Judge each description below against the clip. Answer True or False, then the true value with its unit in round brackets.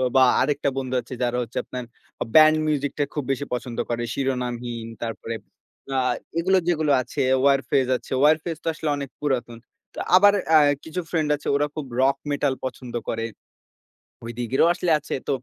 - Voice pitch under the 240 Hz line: True (135 Hz)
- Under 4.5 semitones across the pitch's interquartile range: True (3.7 semitones)